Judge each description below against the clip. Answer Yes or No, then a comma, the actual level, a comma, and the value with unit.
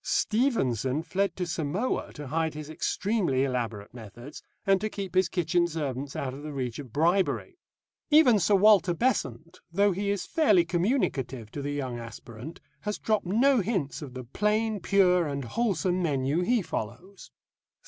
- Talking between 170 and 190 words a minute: No, average, 160 wpm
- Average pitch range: No, wide, 6.7 semitones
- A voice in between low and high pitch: Yes, medium, 170 Hz